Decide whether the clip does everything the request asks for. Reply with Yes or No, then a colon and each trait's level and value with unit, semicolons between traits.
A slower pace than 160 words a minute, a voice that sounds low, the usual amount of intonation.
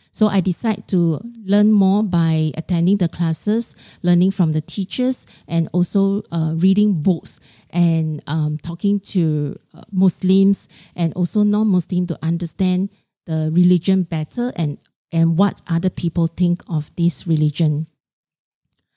No: slow, 135 wpm; medium, 175 Hz; average, 3.0 semitones